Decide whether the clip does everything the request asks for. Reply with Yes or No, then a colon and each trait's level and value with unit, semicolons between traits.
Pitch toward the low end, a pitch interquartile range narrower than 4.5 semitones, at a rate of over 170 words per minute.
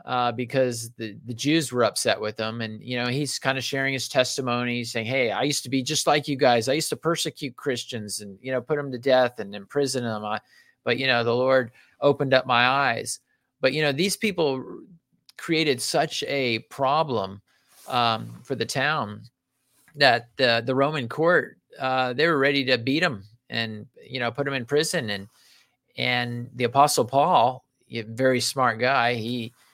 Yes: low, 130 Hz; average, 3.0 semitones; average, 190 wpm